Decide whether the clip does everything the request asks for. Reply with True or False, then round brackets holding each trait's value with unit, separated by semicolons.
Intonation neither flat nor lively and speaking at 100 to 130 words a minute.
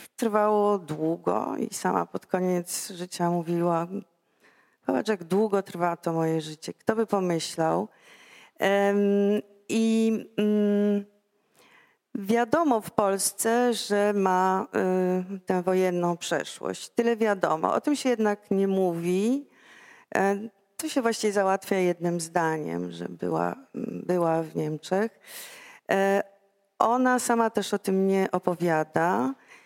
True (3.7 semitones; 115 wpm)